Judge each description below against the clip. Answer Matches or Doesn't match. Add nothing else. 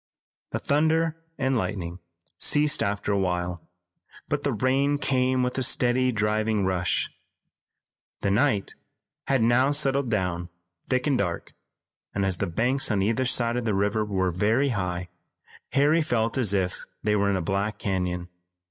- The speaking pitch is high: Doesn't match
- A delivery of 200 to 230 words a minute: Doesn't match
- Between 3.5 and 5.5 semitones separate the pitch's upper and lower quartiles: Matches